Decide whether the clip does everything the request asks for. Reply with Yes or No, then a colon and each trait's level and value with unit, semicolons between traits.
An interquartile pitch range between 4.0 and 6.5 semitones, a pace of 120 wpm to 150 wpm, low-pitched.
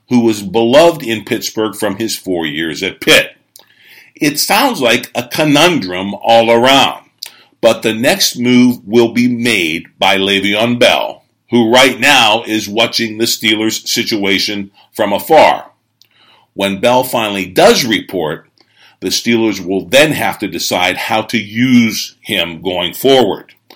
No: average, 3.1 semitones; average, 140 wpm; low, 115 Hz